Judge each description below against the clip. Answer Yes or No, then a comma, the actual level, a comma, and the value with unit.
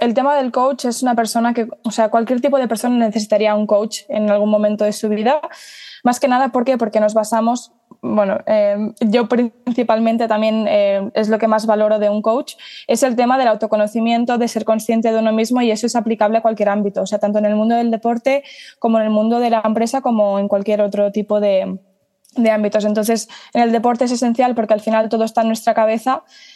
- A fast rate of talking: Yes, fast, 225 wpm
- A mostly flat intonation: Yes, narrow, 2.3 semitones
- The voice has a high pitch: Yes, high, 225 Hz